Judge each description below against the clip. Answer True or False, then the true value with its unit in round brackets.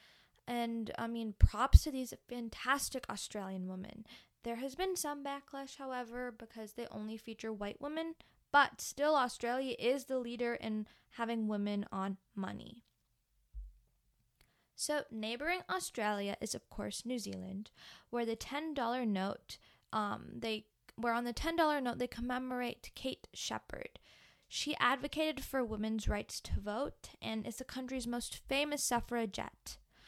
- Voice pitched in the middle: False (240 Hz)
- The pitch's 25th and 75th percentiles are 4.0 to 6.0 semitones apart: False (3.4 semitones)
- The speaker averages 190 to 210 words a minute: False (140 wpm)